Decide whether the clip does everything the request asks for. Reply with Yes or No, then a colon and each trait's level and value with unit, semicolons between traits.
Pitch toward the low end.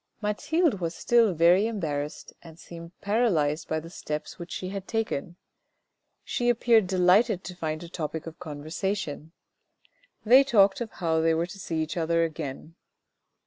No: medium, 175 Hz